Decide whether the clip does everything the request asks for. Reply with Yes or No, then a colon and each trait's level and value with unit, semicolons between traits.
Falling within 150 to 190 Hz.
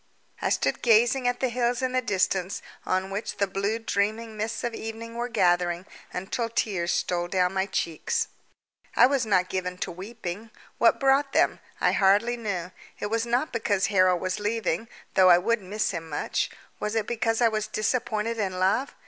No: high, 215 Hz